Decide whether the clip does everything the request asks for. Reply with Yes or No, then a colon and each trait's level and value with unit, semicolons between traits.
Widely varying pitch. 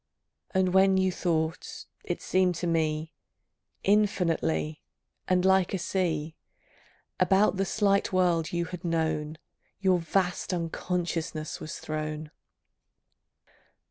No: average, 2.9 semitones